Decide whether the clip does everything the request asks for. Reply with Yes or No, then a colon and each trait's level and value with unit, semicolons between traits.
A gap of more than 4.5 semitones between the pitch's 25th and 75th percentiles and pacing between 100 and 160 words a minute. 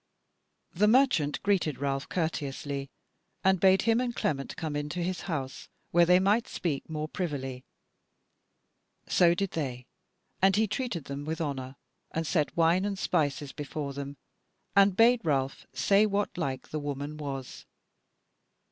Yes: average, 5.3 semitones; average, 140 wpm